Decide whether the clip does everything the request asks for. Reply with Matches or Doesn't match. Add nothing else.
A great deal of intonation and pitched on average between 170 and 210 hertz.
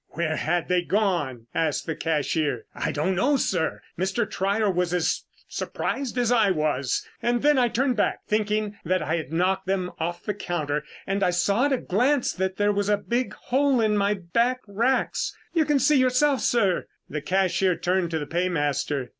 Matches